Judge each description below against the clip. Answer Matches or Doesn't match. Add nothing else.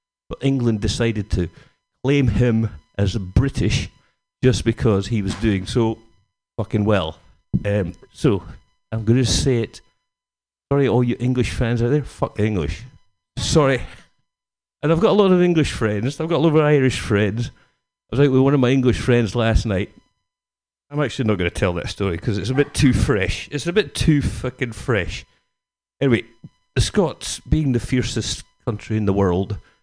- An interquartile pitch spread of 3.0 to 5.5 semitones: Matches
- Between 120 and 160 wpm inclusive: Doesn't match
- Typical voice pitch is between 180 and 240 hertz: Doesn't match